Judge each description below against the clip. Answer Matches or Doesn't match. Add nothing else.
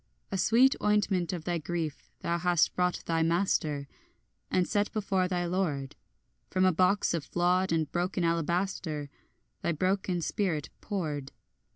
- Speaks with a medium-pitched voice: Matches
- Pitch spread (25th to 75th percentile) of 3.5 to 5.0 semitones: Doesn't match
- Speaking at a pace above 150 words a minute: Doesn't match